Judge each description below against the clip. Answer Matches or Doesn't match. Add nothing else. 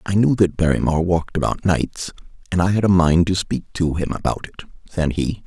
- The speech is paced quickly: Matches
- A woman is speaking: Doesn't match